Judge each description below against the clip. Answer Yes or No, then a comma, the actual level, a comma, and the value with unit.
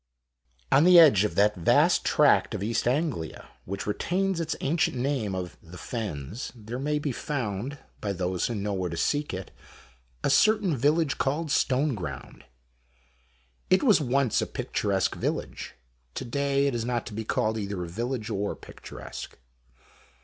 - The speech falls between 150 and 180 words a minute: Yes, average, 160 wpm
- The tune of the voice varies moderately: No, wide, 6.4 semitones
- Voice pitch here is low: Yes, low, 120 Hz